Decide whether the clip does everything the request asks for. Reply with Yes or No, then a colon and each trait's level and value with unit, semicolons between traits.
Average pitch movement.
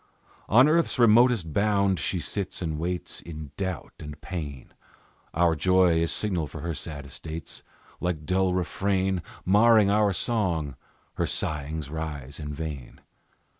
Yes: average, 4.3 semitones